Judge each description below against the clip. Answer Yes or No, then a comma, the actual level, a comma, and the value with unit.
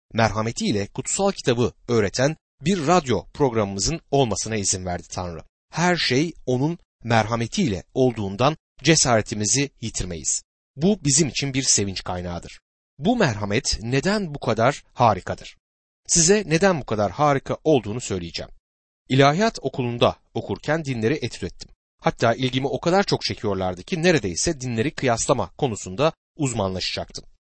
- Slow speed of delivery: No, average, 120 wpm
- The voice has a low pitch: Yes, low, 125 Hz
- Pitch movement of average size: No, wide, 6.7 semitones